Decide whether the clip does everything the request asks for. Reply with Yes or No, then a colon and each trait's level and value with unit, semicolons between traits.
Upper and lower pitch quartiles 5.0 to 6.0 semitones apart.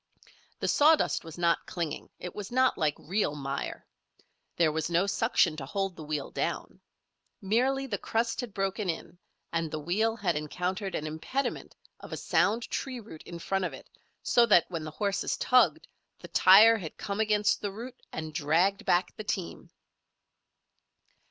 Yes: average, 5.3 semitones